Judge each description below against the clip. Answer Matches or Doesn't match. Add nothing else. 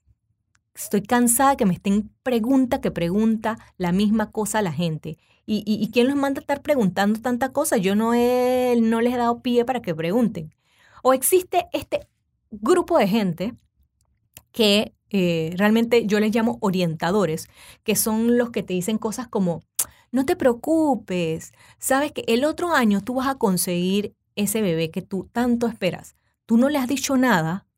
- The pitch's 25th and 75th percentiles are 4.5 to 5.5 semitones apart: Matches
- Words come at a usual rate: Matches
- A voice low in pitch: Doesn't match